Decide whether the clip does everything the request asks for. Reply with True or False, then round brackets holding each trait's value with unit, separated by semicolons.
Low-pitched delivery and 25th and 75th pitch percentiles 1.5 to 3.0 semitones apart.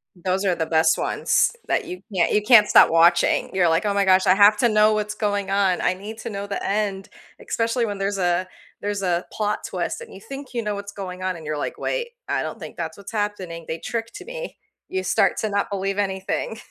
False (200 Hz; 2.4 semitones)